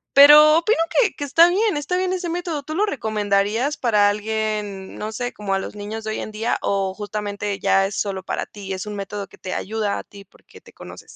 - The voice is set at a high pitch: Yes, high, 215 Hz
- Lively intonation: Yes, wide, 6.3 semitones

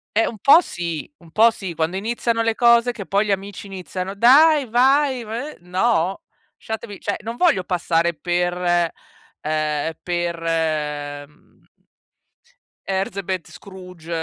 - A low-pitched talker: No, high, 190 Hz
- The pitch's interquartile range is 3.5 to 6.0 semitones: Yes, average, 5.3 semitones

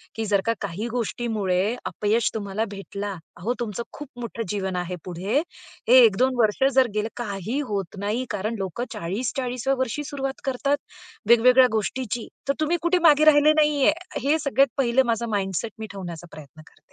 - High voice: Yes, high, 230 Hz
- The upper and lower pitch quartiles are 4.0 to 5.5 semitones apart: Yes, average, 4.6 semitones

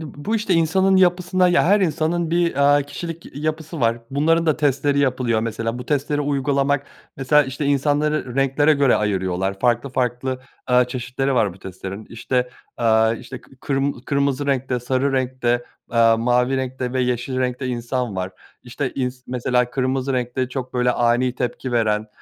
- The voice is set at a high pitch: No, low, 130 Hz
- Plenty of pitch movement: No, average, 2.9 semitones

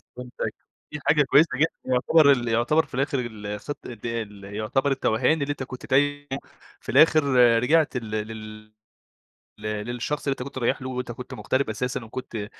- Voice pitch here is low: Yes, low, 125 Hz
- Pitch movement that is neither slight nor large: Yes, average, 4.2 semitones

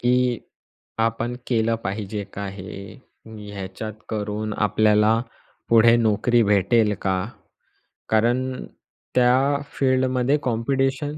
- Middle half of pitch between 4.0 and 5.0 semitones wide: No, average, 3.2 semitones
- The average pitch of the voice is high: No, low, 115 Hz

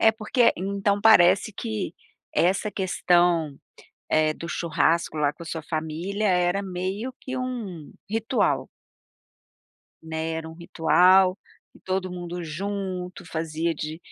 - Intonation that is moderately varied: Yes, average, 3.5 semitones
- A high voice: No, medium, 180 Hz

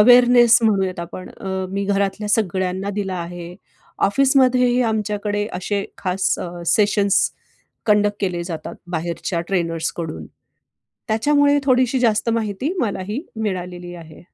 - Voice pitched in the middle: No, high, 200 Hz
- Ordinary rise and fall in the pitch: Yes, average, 4.0 semitones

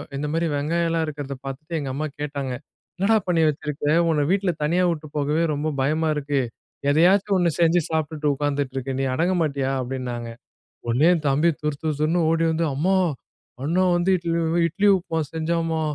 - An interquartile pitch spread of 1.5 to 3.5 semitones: Yes, average, 2.8 semitones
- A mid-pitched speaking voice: Yes, medium, 155 Hz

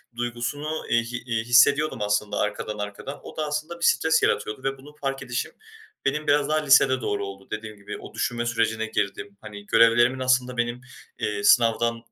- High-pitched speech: No, low, 120 Hz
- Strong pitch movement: No, average, 4.3 semitones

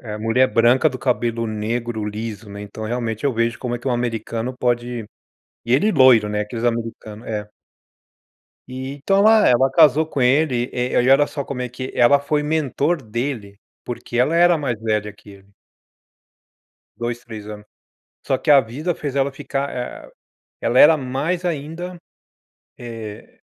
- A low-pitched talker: Yes, low, 125 Hz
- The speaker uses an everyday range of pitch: Yes, average, 3.8 semitones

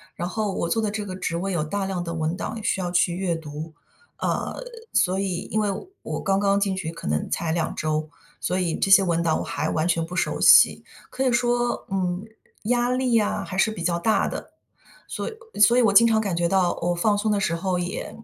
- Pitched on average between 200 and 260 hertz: No, medium, 185 Hz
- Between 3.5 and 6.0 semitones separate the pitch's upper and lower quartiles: Yes, average, 3.8 semitones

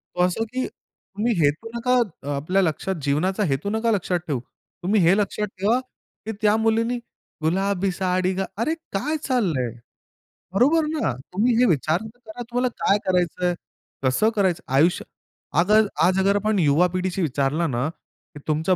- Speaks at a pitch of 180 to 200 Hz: Yes, high, 190 Hz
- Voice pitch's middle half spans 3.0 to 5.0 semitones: Yes, average, 4.7 semitones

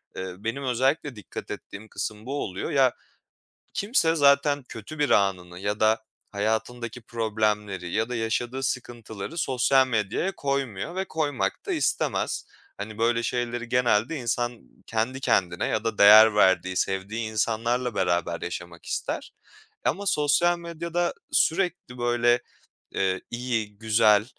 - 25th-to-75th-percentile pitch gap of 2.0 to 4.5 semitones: Yes, average, 4.2 semitones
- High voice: No, low, 115 Hz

